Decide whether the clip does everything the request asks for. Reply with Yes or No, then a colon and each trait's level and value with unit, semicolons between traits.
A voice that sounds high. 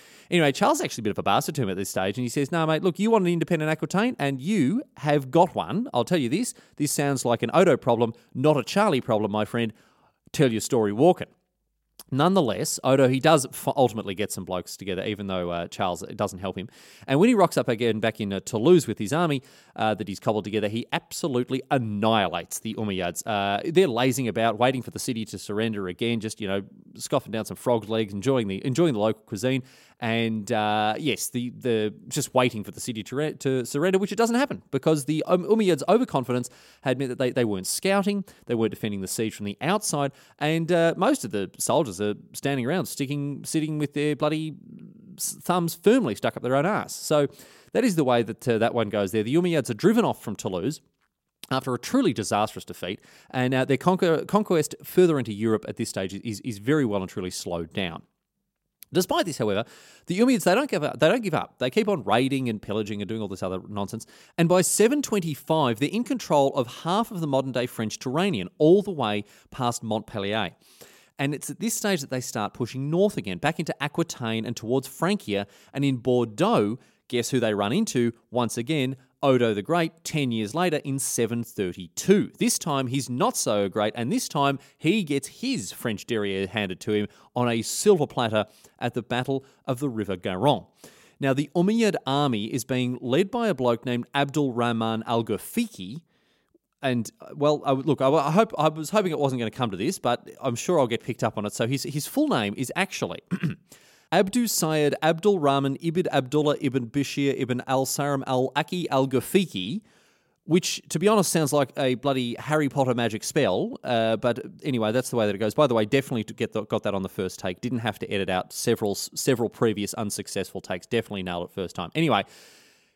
No: low, 130 Hz